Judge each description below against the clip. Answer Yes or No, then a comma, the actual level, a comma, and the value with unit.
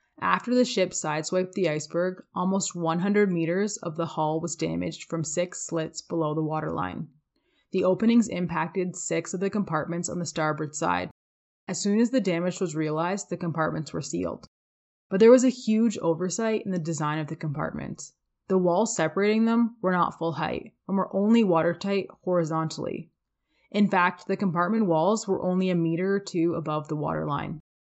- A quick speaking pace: No, average, 175 wpm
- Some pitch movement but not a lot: Yes, average, 3.5 semitones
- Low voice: No, medium, 175 Hz